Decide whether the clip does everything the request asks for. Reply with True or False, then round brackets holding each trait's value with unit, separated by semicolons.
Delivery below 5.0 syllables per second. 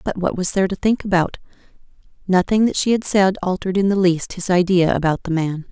False (6.0 syllables/s)